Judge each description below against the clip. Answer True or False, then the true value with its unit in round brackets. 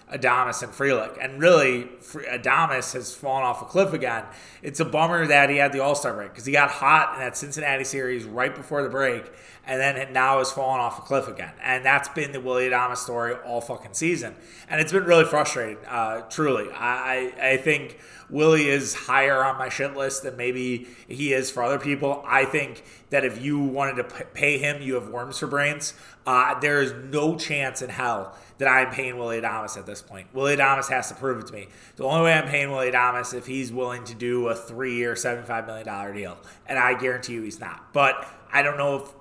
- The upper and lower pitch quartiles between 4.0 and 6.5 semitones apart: False (2.5 semitones)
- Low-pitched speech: True (130 Hz)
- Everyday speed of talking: False (220 wpm)